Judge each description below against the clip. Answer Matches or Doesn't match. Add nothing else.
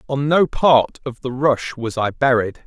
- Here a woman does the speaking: Doesn't match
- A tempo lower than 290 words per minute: Matches